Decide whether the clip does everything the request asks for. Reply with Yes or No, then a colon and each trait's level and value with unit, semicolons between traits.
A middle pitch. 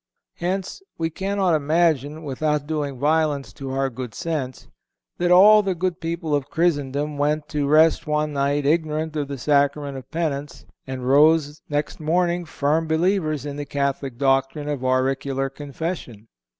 Yes: medium, 150 Hz